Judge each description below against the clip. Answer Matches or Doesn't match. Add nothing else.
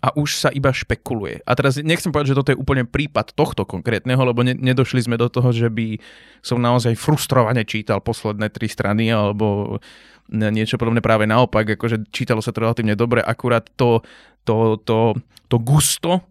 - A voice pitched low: Matches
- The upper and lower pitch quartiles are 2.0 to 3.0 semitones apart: Matches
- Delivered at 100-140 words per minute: Doesn't match